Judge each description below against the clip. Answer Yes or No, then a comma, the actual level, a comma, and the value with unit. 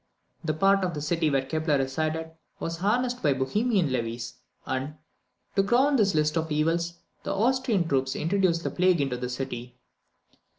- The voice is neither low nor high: Yes, medium, 160 Hz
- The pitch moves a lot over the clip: Yes, wide, 6.3 semitones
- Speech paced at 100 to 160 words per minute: No, average, 170 wpm